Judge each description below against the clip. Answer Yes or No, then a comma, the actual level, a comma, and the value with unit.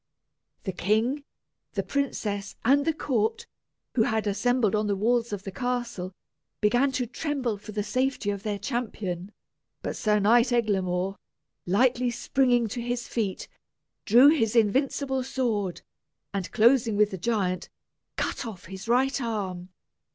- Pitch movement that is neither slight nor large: Yes, average, 3.7 semitones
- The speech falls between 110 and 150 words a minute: Yes, average, 140 wpm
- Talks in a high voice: Yes, high, 225 Hz